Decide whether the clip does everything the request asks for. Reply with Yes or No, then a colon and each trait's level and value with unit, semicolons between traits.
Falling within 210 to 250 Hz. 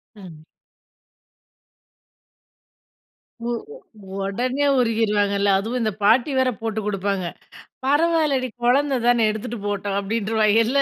Yes: high, 225 Hz